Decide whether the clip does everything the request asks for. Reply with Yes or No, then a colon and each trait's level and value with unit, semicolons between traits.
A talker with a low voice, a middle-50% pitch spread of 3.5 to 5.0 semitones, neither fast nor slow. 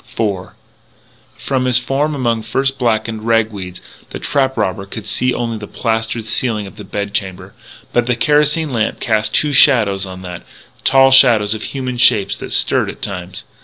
Yes: low, 115 Hz; average, 4.0 semitones; average, 175 wpm